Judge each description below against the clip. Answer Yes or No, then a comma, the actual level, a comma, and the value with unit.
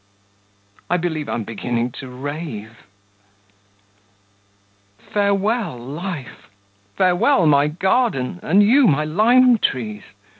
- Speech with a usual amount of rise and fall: No, wide, 8.0 semitones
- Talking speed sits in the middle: No, slow, 90 wpm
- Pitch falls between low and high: Yes, medium, 160 Hz